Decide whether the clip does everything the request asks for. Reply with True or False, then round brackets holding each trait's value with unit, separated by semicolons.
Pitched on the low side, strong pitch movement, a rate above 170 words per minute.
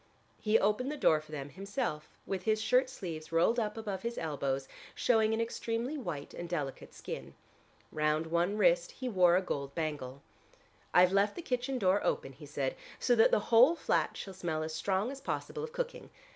False (190 Hz; 6.7 semitones; 190 wpm)